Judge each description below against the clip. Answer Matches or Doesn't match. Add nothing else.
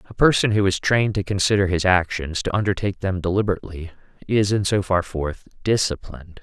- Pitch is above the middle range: Doesn't match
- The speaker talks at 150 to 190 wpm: Matches